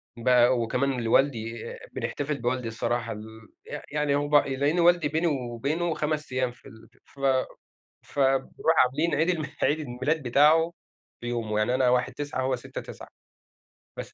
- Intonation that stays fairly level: No, average, 3.7 semitones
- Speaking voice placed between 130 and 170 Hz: Yes, low, 135 Hz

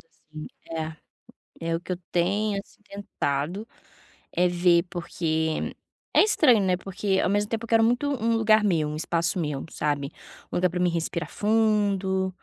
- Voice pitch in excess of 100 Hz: Yes, medium, 185 Hz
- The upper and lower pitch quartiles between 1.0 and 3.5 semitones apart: No, average, 4.2 semitones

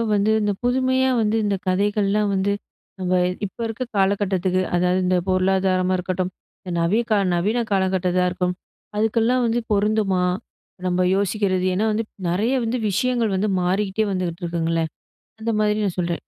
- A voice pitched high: Yes, high, 195 Hz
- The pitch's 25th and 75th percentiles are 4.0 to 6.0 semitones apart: No, average, 2.8 semitones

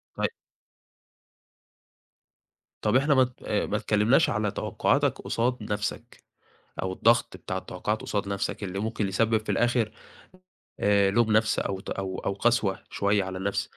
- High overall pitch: No, low, 105 Hz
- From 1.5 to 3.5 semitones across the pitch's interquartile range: Yes, average, 2.7 semitones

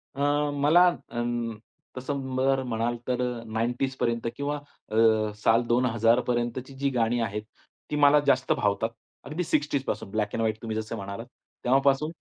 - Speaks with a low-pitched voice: Yes, low, 120 Hz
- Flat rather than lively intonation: No, average, 3.3 semitones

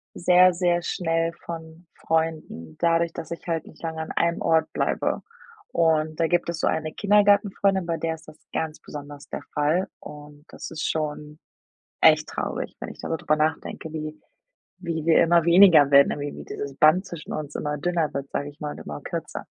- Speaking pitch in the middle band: Yes, medium, 160 Hz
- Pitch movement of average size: No, narrow, 2.0 semitones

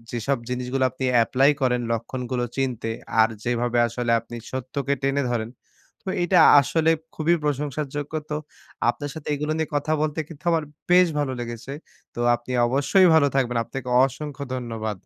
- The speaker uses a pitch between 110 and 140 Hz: Yes, low, 135 Hz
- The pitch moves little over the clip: No, average, 3.4 semitones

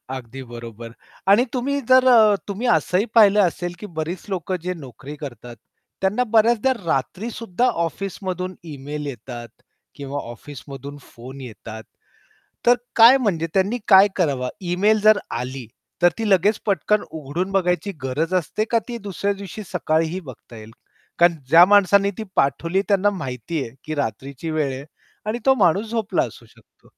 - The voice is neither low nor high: Yes, medium, 175 Hz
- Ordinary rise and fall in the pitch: No, wide, 6.9 semitones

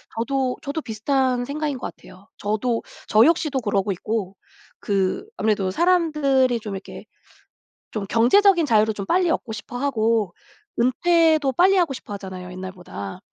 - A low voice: No, high, 235 Hz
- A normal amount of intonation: No, wide, 6.2 semitones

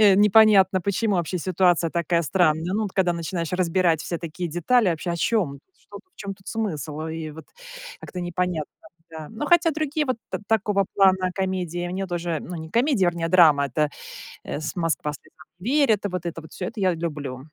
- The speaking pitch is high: No, medium, 180 Hz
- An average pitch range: Yes, average, 3.4 semitones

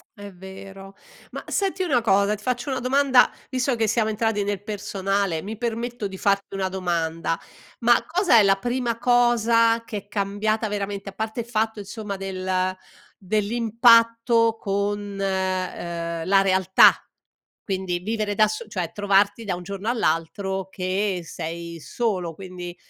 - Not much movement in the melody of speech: No, average, 3.3 semitones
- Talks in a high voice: Yes, high, 205 Hz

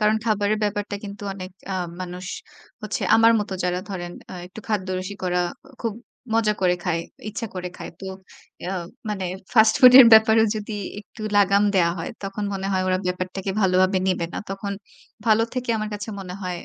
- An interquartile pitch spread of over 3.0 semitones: No, narrow, 2.6 semitones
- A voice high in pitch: Yes, high, 200 Hz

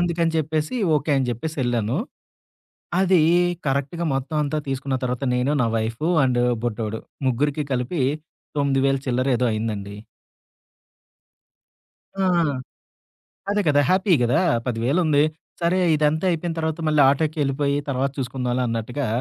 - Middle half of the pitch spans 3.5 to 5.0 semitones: Yes, average, 4.1 semitones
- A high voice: No, medium, 140 Hz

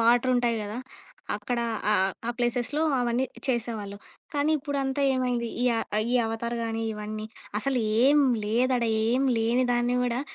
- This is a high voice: Yes, high, 240 Hz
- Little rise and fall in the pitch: Yes, narrow, 2.2 semitones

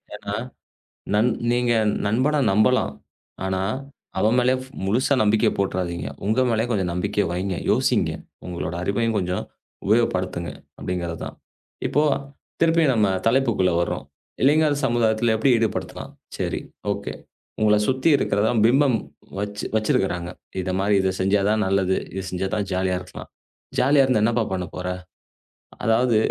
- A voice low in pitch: Yes, low, 105 Hz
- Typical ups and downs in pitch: Yes, average, 4.4 semitones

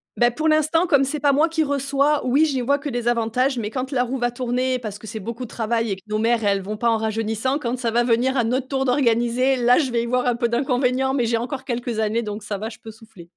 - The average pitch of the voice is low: No, high, 245 Hz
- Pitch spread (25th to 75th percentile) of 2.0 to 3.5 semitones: Yes, average, 2.8 semitones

